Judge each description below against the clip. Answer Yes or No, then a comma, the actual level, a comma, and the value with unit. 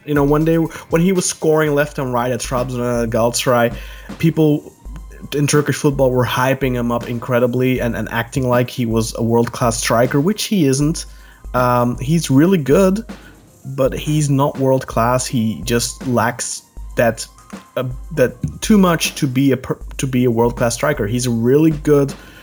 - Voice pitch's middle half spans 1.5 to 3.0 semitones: No, average, 3.8 semitones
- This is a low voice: Yes, low, 130 Hz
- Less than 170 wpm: No, average, 180 wpm